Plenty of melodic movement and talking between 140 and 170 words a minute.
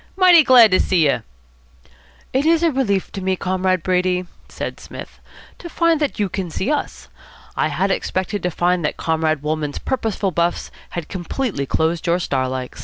No: wide, 6.8 semitones; average, 180 wpm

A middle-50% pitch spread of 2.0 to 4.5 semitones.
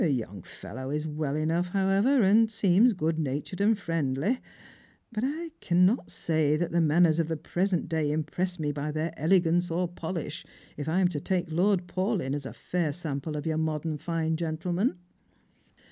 Yes: average, 3.4 semitones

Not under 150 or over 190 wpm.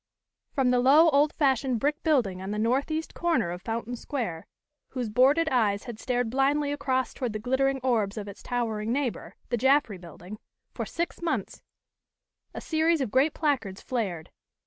Yes: average, 170 wpm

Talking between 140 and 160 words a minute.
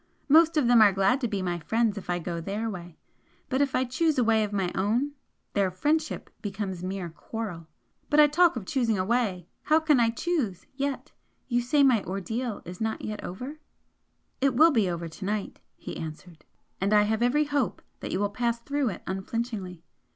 No: average, 200 wpm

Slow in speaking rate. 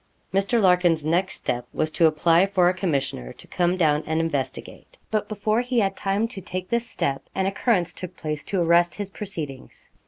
No: average, 190 wpm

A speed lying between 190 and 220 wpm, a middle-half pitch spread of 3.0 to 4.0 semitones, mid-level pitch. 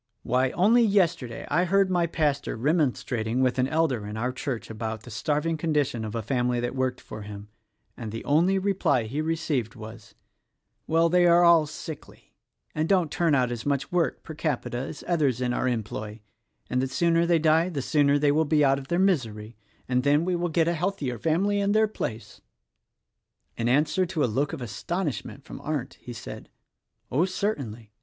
No: average, 195 wpm; wide, 5.6 semitones; medium, 145 Hz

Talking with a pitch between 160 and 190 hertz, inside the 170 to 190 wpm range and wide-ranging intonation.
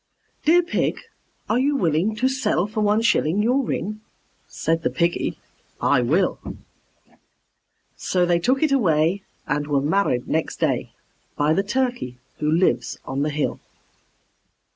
No: medium, 185 Hz; average, 140 wpm; wide, 7.6 semitones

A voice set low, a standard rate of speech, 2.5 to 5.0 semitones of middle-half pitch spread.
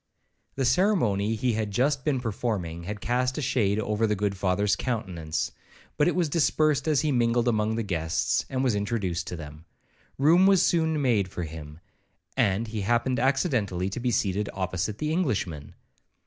No: low, 110 Hz; average, 170 wpm; wide, 5.4 semitones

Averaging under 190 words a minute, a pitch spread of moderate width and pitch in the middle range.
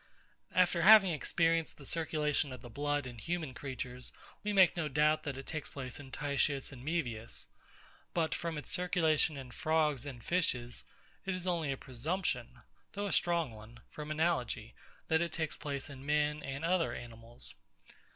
Yes: average, 170 wpm; average, 4.1 semitones; medium, 150 Hz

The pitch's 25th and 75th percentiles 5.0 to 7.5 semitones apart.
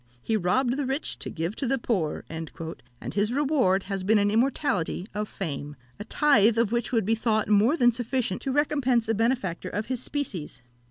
Yes: average, 5.3 semitones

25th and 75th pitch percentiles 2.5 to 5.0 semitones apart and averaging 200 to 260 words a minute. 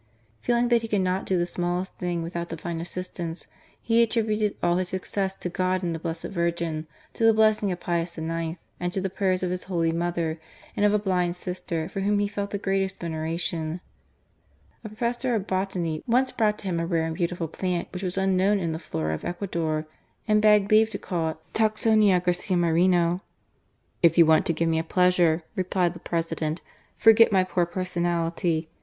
Yes: average, 2.9 semitones; fast, 205 wpm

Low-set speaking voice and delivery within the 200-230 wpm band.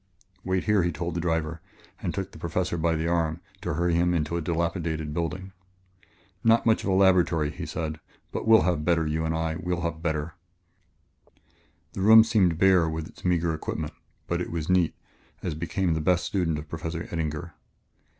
No: very low, 85 Hz; average, 190 wpm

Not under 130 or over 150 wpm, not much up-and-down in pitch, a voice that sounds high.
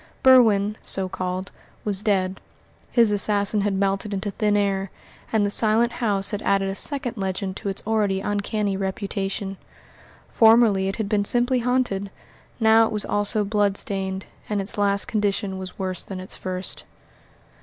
No: average, 160 wpm; narrow, 1.9 semitones; high, 200 Hz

